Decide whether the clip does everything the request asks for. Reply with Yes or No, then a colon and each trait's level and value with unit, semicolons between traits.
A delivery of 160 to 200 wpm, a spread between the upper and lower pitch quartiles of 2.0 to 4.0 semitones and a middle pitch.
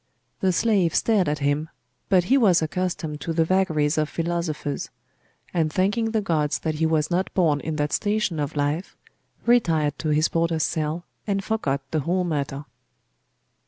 Yes: average, 165 wpm; average, 3.6 semitones; medium, 165 Hz